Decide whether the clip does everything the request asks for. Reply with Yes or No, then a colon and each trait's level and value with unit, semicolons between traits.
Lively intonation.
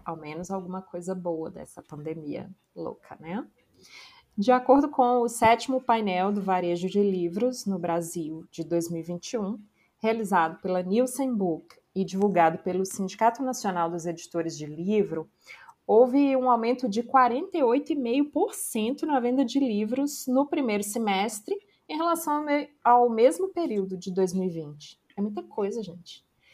Yes: wide, 6.4 semitones